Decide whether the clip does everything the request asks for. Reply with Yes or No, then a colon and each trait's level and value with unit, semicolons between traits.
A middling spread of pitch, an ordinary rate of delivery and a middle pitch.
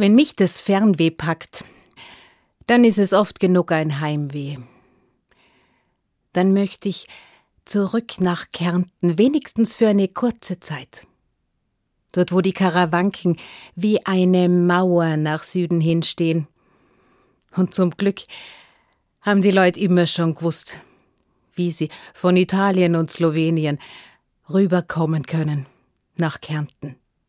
No: average, 3.2 semitones; slow, 115 wpm; medium, 180 Hz